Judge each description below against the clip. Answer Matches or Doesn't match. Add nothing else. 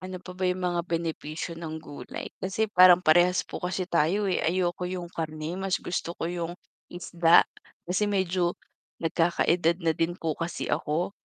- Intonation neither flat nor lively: Doesn't match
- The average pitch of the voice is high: Doesn't match